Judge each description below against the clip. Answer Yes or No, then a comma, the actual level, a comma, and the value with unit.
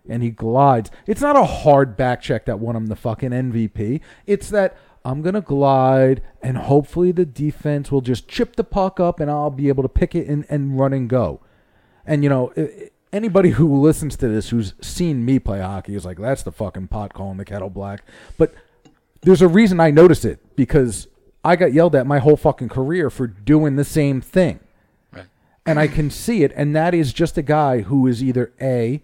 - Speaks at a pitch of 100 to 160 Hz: Yes, medium, 140 Hz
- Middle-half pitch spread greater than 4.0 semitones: Yes, average, 4.7 semitones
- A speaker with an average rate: No, fast, 210 wpm